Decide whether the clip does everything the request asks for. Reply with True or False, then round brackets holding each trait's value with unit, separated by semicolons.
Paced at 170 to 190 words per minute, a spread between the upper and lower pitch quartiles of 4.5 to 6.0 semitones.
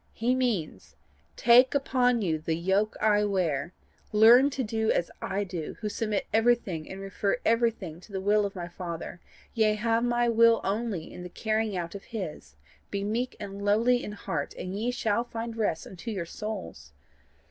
False (180 wpm; 4.0 semitones)